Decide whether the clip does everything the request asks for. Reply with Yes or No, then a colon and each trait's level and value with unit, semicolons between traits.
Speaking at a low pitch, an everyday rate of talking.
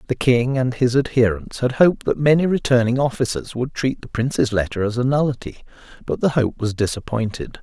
Yes: low, 125 Hz; average, 190 wpm